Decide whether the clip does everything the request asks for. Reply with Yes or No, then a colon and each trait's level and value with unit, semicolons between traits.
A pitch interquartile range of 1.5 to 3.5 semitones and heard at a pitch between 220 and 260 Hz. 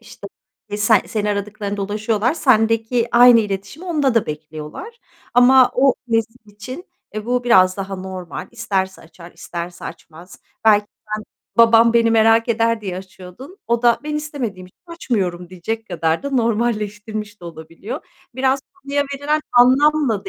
No: average, 4.3 semitones; high, 225 Hz